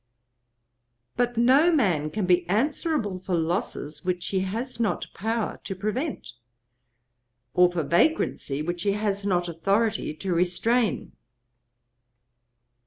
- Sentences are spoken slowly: Yes, slow, 115 wpm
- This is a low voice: No, high, 195 Hz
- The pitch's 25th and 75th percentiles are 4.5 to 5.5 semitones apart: Yes, average, 4.8 semitones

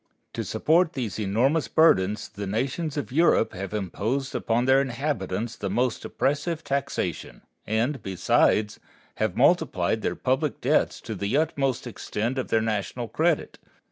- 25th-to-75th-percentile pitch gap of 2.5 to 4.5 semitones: No, average, 4.9 semitones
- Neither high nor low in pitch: No, low, 125 Hz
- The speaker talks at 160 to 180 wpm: No, average, 140 wpm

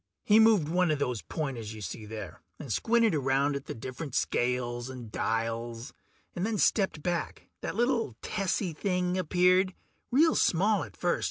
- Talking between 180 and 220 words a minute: No, average, 165 wpm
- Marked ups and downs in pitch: Yes, wide, 7.8 semitones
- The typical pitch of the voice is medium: Yes, medium, 155 Hz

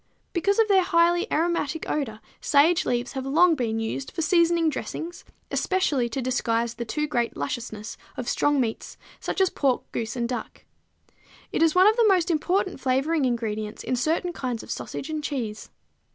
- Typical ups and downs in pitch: No, wide, 6.1 semitones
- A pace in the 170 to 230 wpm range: Yes, average, 180 wpm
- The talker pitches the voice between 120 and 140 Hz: No, very high, 285 Hz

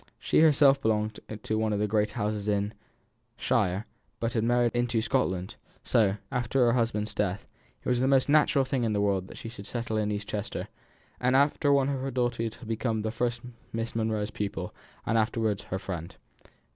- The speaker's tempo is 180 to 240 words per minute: Yes, average, 195 wpm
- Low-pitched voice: Yes, low, 110 Hz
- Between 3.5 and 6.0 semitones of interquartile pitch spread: No, average, 2.9 semitones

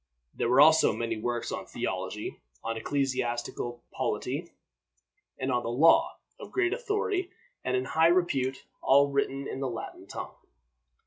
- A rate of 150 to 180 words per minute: No, average, 140 wpm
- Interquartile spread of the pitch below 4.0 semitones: No, average, 4.9 semitones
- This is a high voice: No, low, 135 Hz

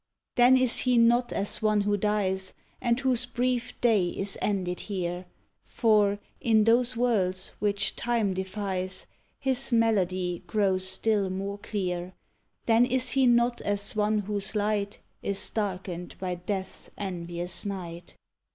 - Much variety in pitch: No, average, 3.7 semitones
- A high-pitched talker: Yes, high, 205 Hz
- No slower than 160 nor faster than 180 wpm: No, slow, 135 wpm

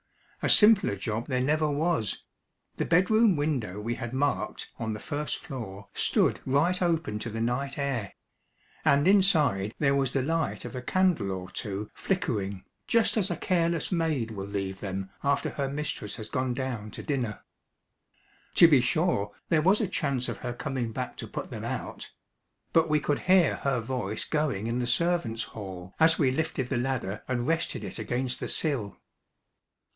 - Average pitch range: No, wide, 6.2 semitones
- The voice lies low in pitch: Yes, low, 130 Hz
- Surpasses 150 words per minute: Yes, average, 175 wpm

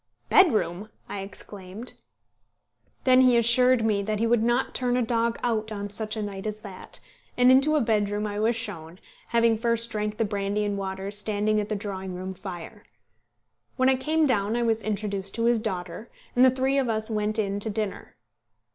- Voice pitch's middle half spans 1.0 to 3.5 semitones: Yes, average, 2.7 semitones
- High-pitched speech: Yes, high, 215 Hz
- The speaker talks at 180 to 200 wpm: Yes, average, 190 wpm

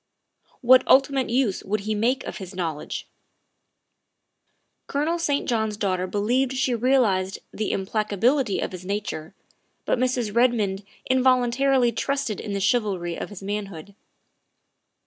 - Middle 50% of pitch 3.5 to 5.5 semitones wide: Yes, average, 4.5 semitones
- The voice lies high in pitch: Yes, high, 220 Hz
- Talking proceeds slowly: Yes, slow, 130 wpm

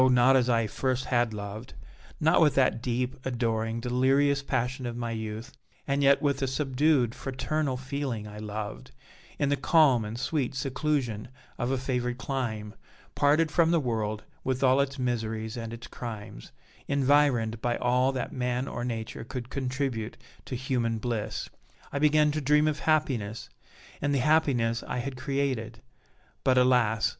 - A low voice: Yes, low, 125 Hz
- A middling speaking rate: Yes, average, 160 wpm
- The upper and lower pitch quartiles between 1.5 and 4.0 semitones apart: Yes, average, 3.3 semitones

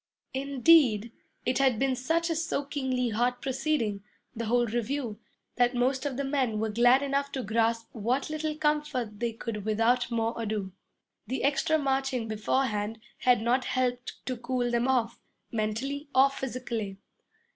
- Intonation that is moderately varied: Yes, average, 3.2 semitones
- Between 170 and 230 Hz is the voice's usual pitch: No, very high, 250 Hz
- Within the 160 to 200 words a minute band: No, average, 150 wpm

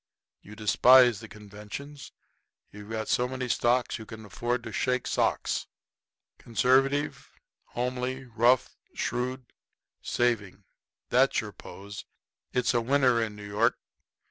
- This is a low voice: Yes, low, 120 Hz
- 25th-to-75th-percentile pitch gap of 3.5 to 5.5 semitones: No, average, 2.9 semitones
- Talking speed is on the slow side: Yes, slow, 120 wpm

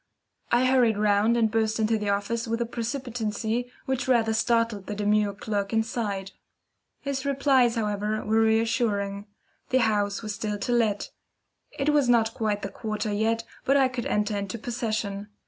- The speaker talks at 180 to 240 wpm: No, average, 165 wpm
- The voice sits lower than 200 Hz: No, high, 220 Hz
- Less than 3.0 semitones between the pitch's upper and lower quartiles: Yes, narrow, 2.4 semitones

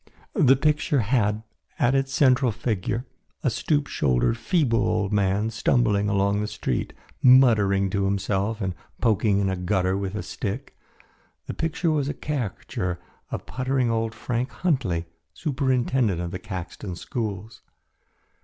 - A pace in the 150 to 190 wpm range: No, average, 140 wpm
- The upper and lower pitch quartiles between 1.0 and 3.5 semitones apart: No, average, 4.7 semitones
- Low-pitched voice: Yes, low, 110 Hz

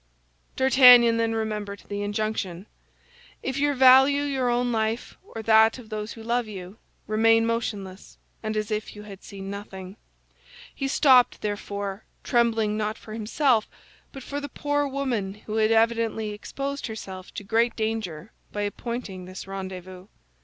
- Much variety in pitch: No, average, 2.9 semitones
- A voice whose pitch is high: Yes, high, 220 Hz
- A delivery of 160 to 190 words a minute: No, average, 150 wpm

